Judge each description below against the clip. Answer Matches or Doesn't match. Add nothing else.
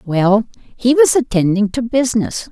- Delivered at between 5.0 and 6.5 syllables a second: Doesn't match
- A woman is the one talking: Matches